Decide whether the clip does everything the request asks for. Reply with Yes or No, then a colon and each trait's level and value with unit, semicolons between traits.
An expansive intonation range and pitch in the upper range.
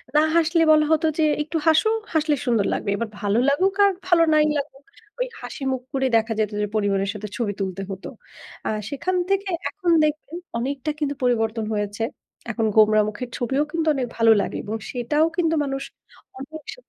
Yes: wide, 6.1 semitones; very high, 270 Hz